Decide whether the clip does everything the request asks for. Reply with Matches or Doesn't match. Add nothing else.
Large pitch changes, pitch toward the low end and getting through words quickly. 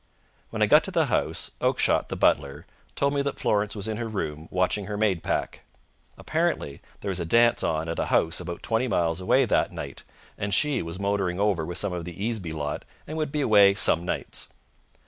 Doesn't match